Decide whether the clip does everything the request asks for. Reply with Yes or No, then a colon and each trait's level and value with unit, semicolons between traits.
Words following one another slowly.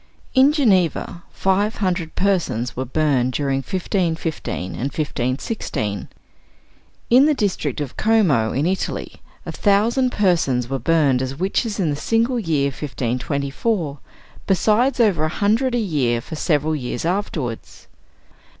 Yes: slow, 130 wpm